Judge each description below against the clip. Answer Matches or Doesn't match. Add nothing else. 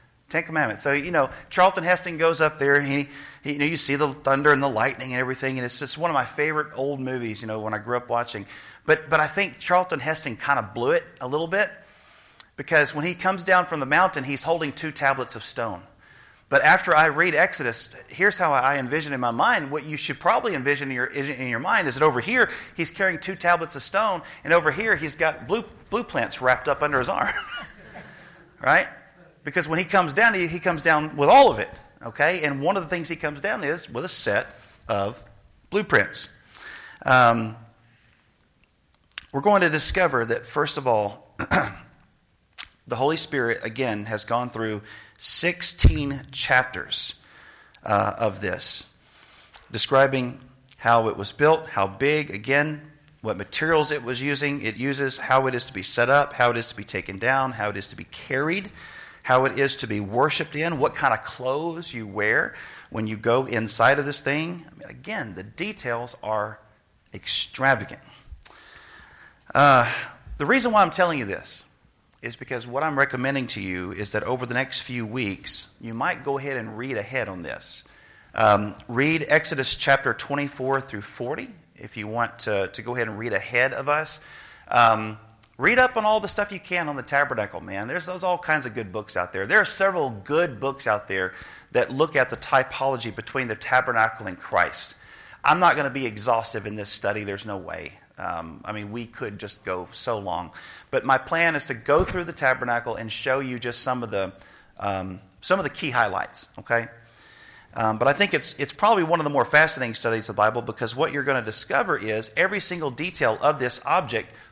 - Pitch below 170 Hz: Matches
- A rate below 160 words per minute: Doesn't match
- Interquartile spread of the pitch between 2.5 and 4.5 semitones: Doesn't match